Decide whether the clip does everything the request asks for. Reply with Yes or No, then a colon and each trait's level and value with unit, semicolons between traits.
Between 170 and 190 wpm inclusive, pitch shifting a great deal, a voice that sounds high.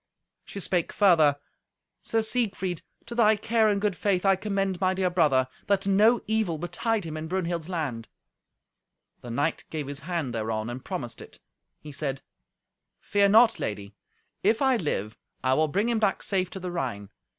No: average, 175 wpm; wide, 6.2 semitones; medium, 180 Hz